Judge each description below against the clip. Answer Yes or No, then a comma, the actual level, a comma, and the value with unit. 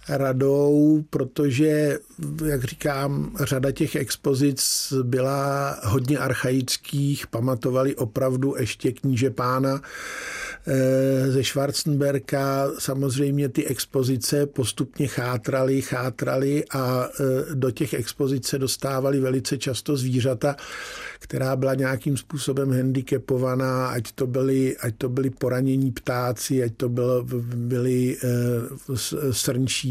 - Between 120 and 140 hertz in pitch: Yes, low, 135 Hz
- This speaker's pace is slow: Yes, slow, 100 wpm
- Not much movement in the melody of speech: Yes, narrow, 1.5 semitones